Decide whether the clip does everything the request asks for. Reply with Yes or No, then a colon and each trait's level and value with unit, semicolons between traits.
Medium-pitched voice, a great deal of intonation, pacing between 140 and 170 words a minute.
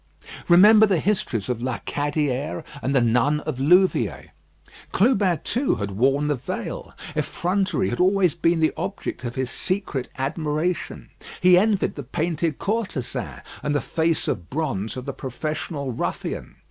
Yes: medium, 155 Hz; wide, 5.7 semitones; average, 145 wpm